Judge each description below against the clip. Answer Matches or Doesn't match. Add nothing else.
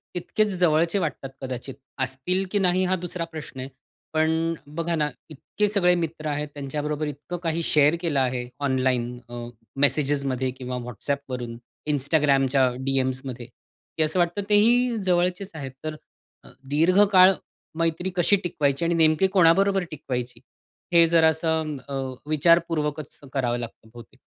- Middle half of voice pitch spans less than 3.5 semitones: Doesn't match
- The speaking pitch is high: Doesn't match